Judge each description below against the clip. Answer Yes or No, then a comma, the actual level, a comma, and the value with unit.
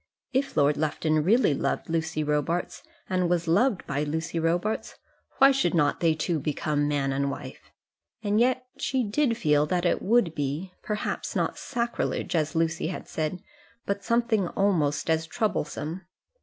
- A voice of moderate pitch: Yes, medium, 165 Hz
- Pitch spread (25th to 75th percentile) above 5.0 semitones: Yes, wide, 5.4 semitones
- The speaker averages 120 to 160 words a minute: Yes, average, 155 wpm